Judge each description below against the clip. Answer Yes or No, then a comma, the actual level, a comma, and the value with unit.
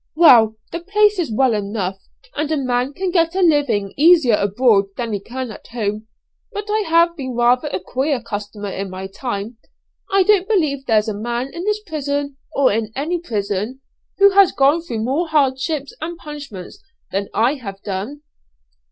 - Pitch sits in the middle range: No, very high, 260 Hz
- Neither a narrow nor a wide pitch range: No, wide, 7.2 semitones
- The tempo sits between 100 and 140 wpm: No, average, 180 wpm